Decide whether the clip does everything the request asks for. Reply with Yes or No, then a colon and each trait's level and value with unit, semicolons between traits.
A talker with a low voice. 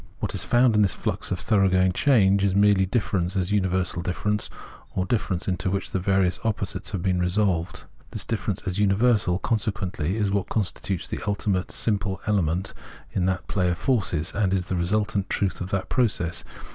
Yes: very low, 95 Hz